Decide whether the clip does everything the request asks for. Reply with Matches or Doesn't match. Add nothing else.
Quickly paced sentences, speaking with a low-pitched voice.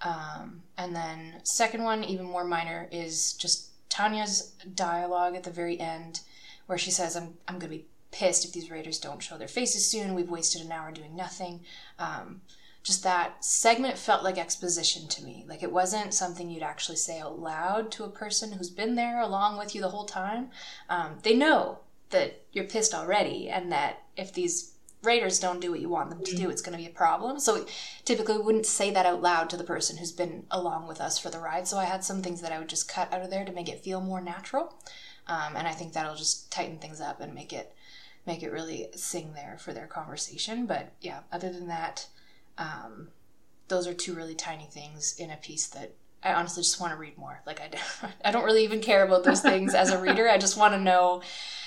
Doesn't match